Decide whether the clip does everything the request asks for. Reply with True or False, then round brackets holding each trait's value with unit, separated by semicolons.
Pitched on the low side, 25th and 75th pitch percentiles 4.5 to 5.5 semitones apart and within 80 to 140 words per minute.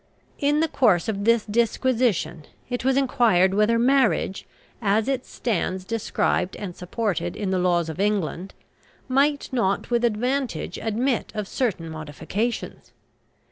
False (215 Hz; 4.9 semitones; 135 wpm)